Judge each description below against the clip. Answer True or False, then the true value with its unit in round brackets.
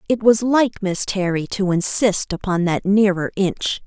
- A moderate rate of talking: True (170 wpm)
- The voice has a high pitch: True (195 Hz)